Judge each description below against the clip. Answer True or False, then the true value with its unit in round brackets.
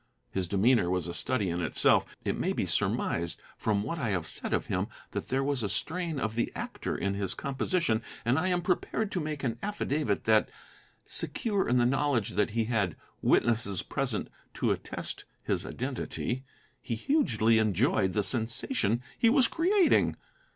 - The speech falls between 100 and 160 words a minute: False (170 wpm)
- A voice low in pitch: True (120 Hz)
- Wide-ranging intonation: True (6.8 semitones)